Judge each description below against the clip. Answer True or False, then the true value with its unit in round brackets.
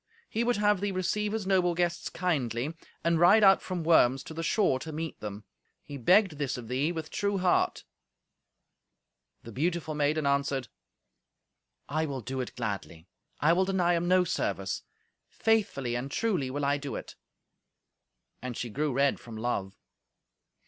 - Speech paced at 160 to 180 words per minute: True (165 wpm)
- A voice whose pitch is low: False (155 Hz)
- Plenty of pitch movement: True (5.8 semitones)